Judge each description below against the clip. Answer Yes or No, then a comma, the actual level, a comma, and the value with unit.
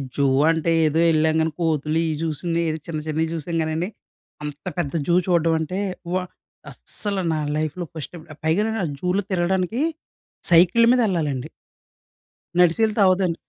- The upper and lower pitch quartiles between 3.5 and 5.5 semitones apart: No, average, 2.7 semitones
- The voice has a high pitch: No, medium, 165 Hz